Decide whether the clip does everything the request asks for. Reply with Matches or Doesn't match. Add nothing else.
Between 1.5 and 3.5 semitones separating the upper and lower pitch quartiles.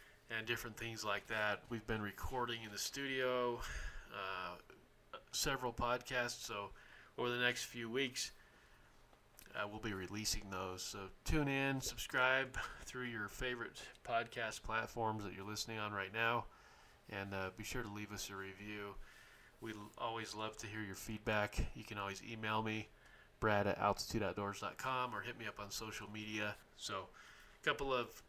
Matches